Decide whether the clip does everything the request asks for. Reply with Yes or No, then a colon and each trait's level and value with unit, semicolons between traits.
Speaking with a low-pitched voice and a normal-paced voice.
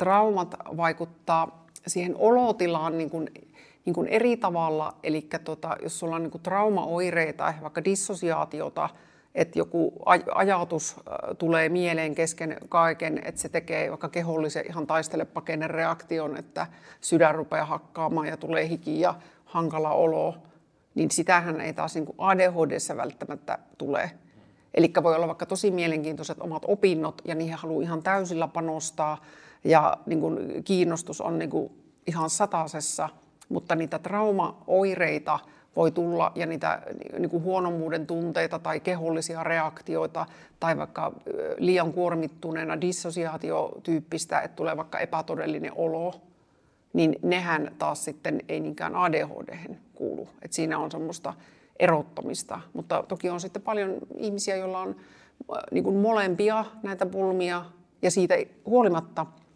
No: medium, 165 Hz; average, 125 wpm